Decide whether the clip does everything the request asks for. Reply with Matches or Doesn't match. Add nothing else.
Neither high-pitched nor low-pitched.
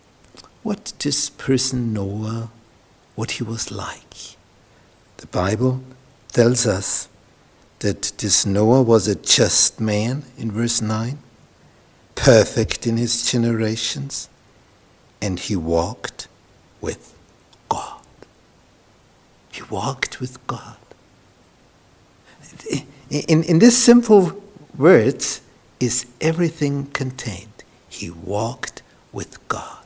Doesn't match